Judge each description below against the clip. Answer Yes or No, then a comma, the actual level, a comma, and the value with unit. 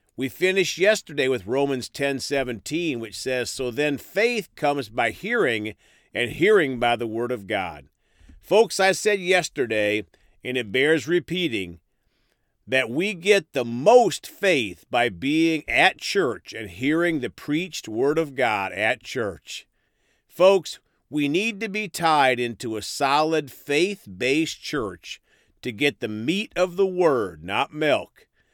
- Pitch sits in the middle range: Yes, medium, 145 Hz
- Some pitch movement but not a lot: No, wide, 6.5 semitones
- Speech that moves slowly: No, average, 145 wpm